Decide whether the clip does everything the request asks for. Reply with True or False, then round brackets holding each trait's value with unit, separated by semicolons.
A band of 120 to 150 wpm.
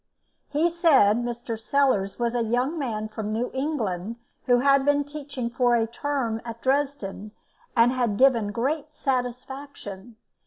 True (145 wpm)